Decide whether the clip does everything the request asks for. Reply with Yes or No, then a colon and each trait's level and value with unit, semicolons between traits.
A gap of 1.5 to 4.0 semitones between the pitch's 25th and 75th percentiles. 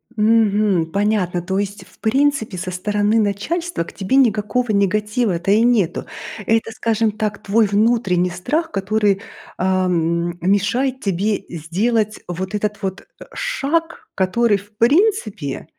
Yes: average, 3.3 semitones